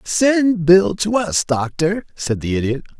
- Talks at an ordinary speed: Yes, average, 160 wpm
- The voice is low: No, medium, 170 Hz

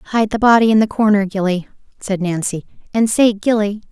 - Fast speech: No, average, 185 wpm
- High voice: Yes, high, 205 Hz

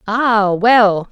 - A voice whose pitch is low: No, high, 215 Hz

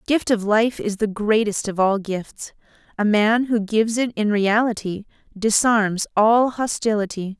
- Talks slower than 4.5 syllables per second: Yes, 4.2 syllables/s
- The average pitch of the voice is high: Yes, high, 215 Hz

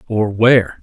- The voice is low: Yes, low, 110 Hz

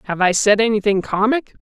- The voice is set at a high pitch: Yes, high, 210 Hz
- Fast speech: No, average, 185 wpm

